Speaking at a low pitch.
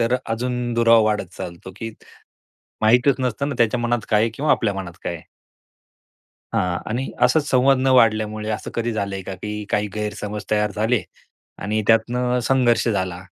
Yes: low, 110 Hz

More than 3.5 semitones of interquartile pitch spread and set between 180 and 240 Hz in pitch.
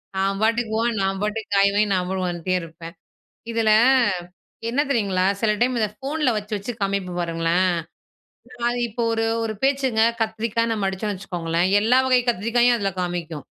Yes: average, 3.9 semitones; high, 205 Hz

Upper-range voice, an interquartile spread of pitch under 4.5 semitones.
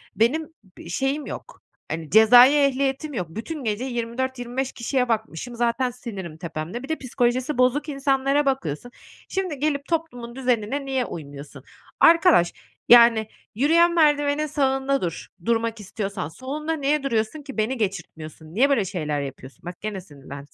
No: high, 245 Hz; wide, 5.4 semitones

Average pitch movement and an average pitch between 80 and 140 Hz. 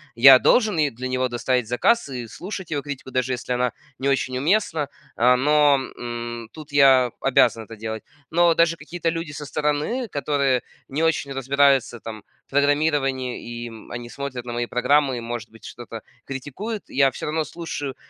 Yes: average, 3.5 semitones; low, 135 Hz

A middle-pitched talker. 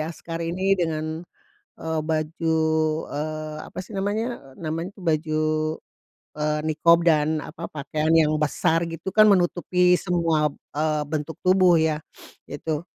Yes: medium, 160 Hz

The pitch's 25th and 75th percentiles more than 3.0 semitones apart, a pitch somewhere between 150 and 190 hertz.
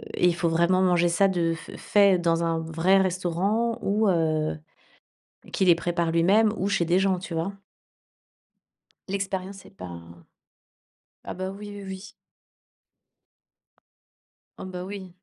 No: average, 2.7 semitones; medium, 185 Hz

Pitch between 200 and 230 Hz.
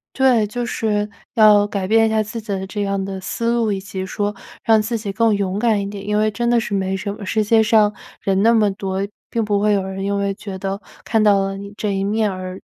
Yes: high, 205 Hz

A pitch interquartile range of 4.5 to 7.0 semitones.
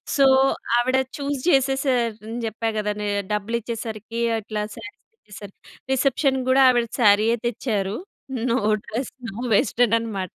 No: average, 3.4 semitones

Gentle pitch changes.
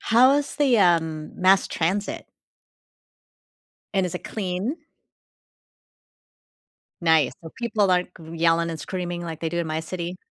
No: average, 3.2 semitones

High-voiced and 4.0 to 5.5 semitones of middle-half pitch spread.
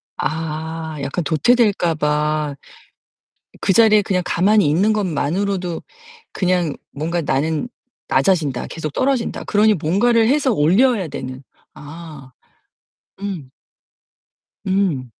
No: medium, 170 Hz; average, 5.1 semitones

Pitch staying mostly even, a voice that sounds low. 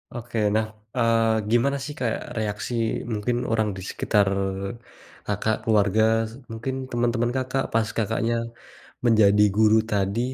Yes: narrow, 2.0 semitones; low, 115 Hz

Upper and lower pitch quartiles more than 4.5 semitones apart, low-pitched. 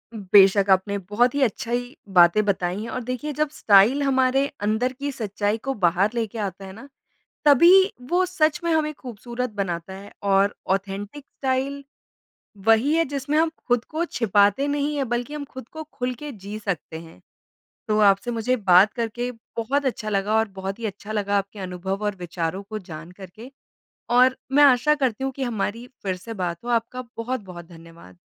No: average, 5.0 semitones; high, 225 Hz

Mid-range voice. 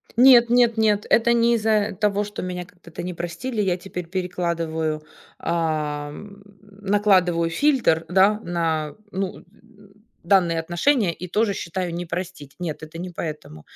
Yes: medium, 180 Hz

